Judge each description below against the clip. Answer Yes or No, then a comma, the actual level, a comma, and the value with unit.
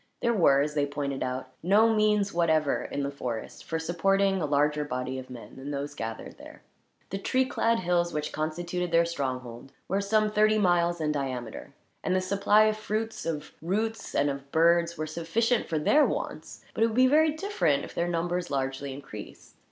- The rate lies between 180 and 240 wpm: Yes, average, 190 wpm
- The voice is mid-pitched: Yes, medium, 170 Hz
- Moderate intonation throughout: No, wide, 6.1 semitones